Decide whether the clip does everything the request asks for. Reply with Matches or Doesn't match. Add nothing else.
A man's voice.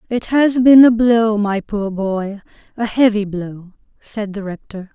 Doesn't match